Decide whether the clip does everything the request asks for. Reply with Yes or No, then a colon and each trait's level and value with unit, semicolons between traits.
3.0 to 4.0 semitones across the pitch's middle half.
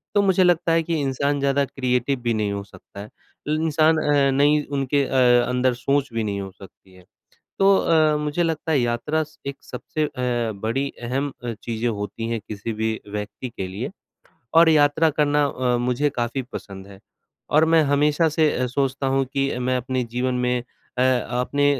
Yes: average, 3.7 semitones